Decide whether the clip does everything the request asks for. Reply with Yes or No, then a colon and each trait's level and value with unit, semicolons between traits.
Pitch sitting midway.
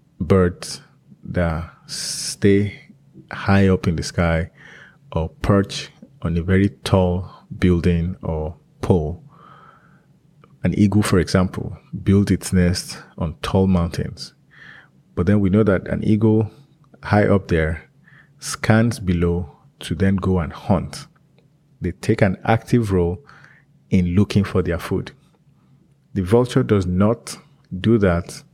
No: very low, 95 Hz